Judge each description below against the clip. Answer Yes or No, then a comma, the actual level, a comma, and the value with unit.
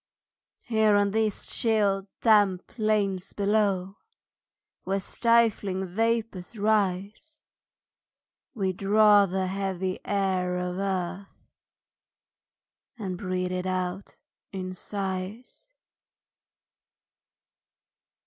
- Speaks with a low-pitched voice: No, high, 195 Hz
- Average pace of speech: No, slow, 80 wpm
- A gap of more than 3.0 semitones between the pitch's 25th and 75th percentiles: No, narrow, 2.4 semitones